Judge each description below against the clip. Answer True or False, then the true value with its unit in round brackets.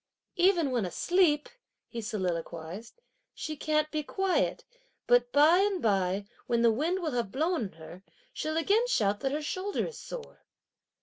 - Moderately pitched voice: False (290 Hz)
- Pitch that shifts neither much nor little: False (8.6 semitones)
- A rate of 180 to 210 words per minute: False (160 wpm)